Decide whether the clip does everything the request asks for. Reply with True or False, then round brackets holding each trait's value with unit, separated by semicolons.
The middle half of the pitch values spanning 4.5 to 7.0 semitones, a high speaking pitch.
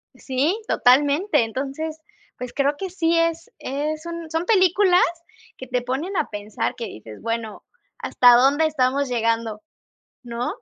True (5.2 semitones; 280 Hz)